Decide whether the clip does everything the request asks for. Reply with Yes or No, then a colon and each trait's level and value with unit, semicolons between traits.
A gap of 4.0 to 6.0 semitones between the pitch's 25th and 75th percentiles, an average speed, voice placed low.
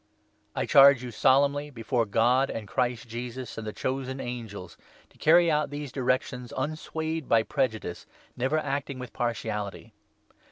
No: average, 3.6 semitones; average, 165 wpm; low, 125 Hz